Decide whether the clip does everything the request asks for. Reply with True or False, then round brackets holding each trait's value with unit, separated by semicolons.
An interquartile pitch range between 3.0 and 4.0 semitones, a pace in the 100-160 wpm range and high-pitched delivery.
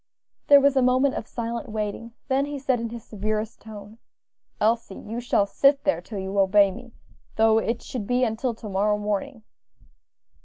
False (3.3 semitones; 180 wpm; 225 Hz)